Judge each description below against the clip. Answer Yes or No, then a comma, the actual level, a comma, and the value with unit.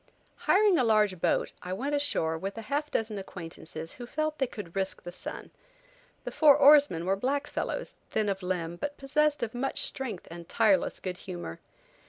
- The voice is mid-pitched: No, high, 215 Hz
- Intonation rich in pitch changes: Yes, wide, 7.8 semitones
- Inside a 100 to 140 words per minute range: No, average, 185 wpm